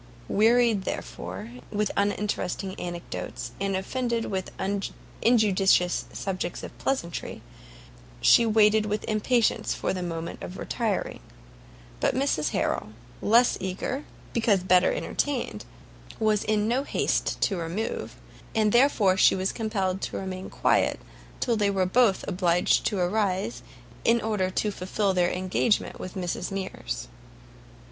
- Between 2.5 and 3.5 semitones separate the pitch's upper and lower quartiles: Yes, average, 3.2 semitones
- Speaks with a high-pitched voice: Yes, high, 195 Hz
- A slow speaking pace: Yes, slow, 125 wpm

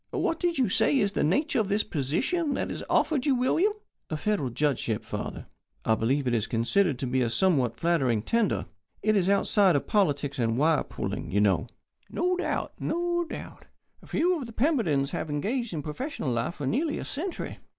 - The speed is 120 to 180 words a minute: No, average, 190 wpm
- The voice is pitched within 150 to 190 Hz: Yes, medium, 185 Hz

